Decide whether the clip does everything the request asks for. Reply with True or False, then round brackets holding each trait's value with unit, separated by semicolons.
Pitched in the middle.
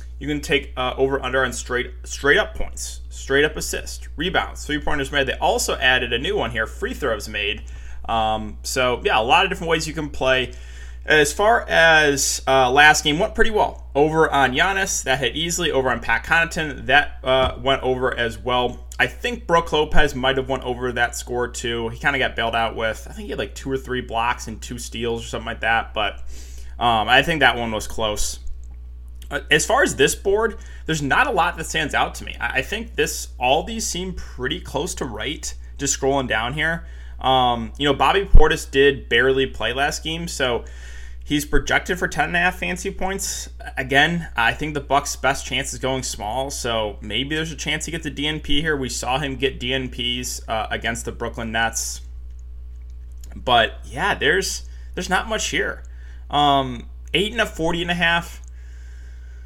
False (125 Hz)